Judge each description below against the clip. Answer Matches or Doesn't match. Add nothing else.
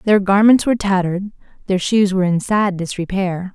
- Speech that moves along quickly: Doesn't match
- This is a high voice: Matches